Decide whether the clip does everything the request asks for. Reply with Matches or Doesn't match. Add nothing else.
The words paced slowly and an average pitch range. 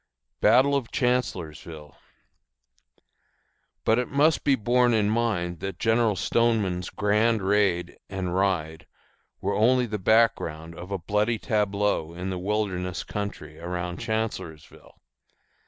Matches